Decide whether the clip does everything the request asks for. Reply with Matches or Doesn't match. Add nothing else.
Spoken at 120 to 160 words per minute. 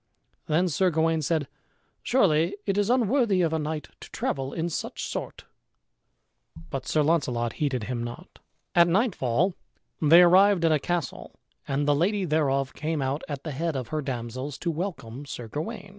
Doesn't match